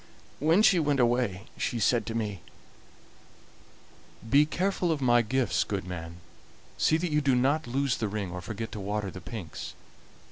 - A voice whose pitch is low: Yes, low, 120 Hz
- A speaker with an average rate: Yes, average, 170 wpm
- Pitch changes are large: Yes, wide, 6.0 semitones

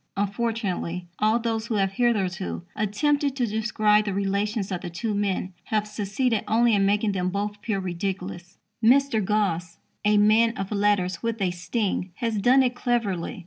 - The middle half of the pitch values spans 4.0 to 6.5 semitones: No, average, 2.8 semitones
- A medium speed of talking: Yes, average, 165 wpm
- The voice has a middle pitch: No, high, 210 Hz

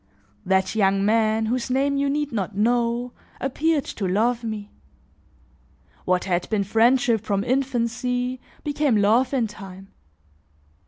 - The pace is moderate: No, slow, 125 wpm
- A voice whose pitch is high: Yes, high, 230 Hz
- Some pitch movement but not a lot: Yes, average, 3.8 semitones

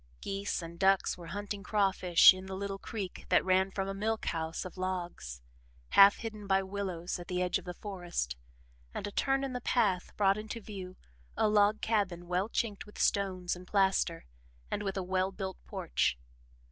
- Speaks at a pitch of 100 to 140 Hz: No, high, 195 Hz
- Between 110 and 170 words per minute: No, average, 185 wpm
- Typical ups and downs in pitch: No, narrow, 2.1 semitones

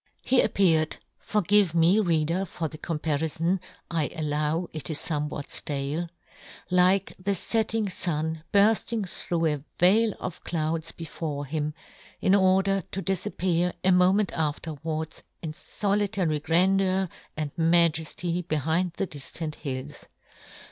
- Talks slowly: Yes, slow, 130 wpm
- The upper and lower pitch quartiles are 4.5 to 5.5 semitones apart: No, average, 3.5 semitones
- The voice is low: No, medium, 170 Hz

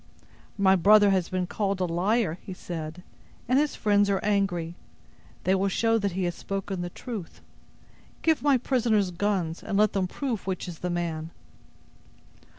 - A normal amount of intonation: Yes, average, 3.0 semitones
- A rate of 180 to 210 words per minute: No, average, 165 wpm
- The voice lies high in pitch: Yes, high, 195 Hz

